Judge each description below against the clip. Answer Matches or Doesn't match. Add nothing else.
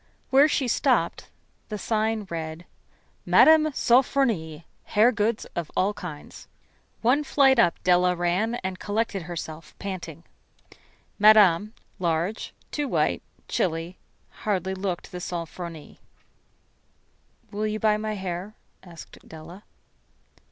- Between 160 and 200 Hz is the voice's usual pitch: Matches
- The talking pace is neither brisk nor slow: Doesn't match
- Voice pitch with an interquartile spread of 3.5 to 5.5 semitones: Matches